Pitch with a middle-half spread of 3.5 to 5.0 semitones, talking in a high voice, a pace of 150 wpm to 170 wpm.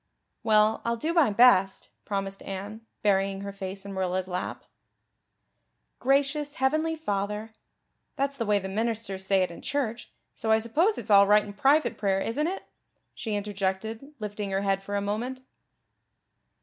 Yes: average, 4.1 semitones; high, 210 Hz; average, 160 wpm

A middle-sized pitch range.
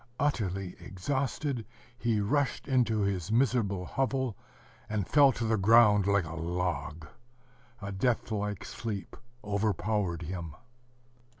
Yes: average, 4.5 semitones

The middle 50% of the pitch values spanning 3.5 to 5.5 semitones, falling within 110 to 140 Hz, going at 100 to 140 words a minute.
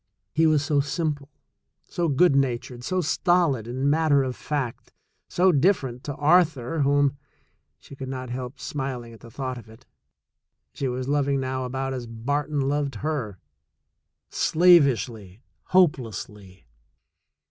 No: average, 3.1 semitones; low, 135 Hz; slow, 135 wpm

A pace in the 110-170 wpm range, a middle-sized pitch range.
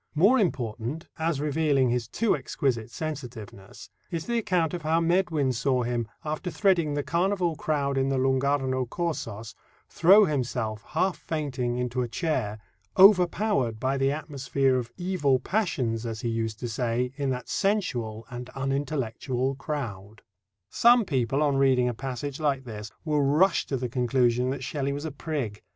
Yes: average, 160 wpm; average, 4.5 semitones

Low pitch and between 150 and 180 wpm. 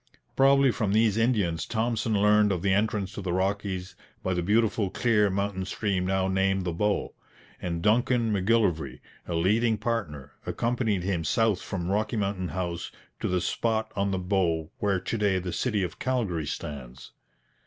Yes: low, 100 Hz; average, 165 wpm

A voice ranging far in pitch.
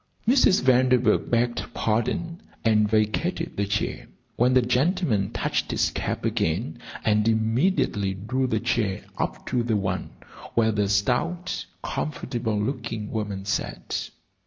No: average, 3.6 semitones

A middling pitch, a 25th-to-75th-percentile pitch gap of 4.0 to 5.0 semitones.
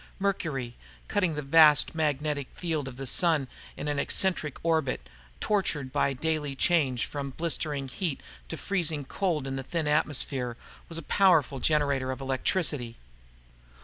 No: medium, 150 Hz; average, 3.5 semitones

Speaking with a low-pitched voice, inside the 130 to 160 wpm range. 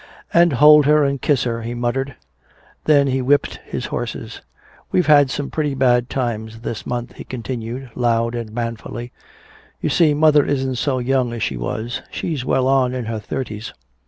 No: low, 130 Hz; average, 175 wpm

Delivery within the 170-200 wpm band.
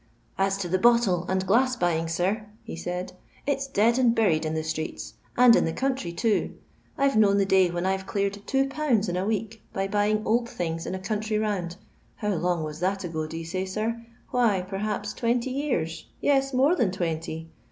Yes: average, 190 wpm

